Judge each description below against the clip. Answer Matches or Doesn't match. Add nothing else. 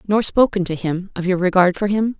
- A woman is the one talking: Matches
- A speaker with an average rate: Doesn't match